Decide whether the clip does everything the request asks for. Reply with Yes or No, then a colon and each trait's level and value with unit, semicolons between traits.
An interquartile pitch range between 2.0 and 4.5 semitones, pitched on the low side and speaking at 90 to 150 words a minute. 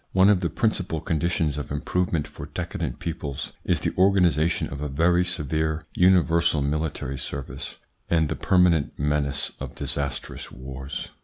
Yes: average, 3.6 semitones; very low, 80 Hz; average, 145 wpm